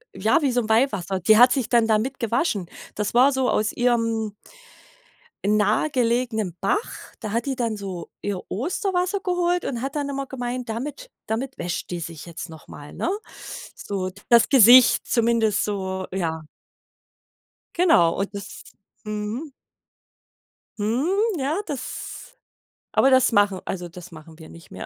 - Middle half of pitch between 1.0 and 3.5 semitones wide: No, average, 5.2 semitones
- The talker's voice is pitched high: Yes, high, 230 Hz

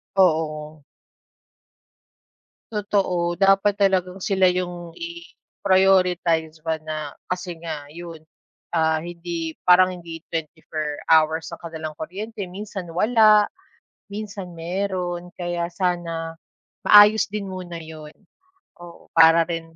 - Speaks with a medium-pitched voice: Yes, medium, 175 Hz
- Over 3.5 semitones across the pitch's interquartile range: No, narrow, 2.5 semitones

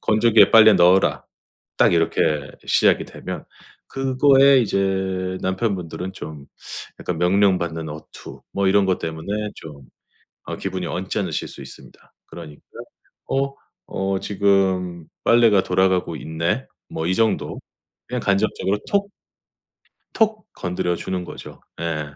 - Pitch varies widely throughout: No, average, 3.7 semitones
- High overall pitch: No, very low, 95 Hz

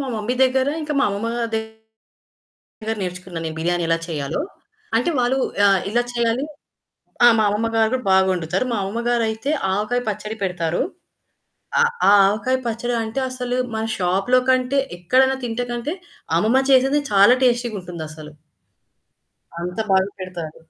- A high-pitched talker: Yes, high, 220 Hz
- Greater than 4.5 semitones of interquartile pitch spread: Yes, average, 4.9 semitones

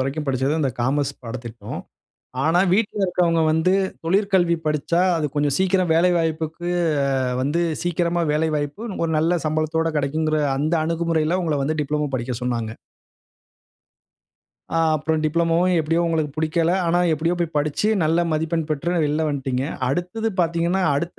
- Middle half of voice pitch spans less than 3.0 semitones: Yes, narrow, 2.6 semitones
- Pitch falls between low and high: Yes, medium, 160 Hz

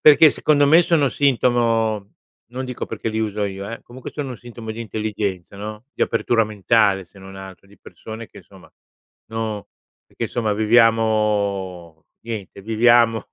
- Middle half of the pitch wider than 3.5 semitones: No, average, 2.8 semitones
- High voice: No, low, 110 Hz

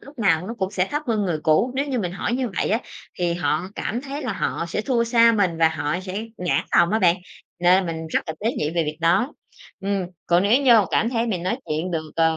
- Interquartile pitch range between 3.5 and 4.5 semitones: No, wide, 5.6 semitones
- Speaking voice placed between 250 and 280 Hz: No, high, 190 Hz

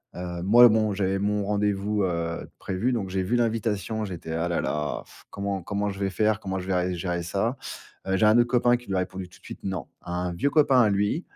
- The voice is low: Yes, low, 100 Hz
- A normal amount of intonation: Yes, average, 3.1 semitones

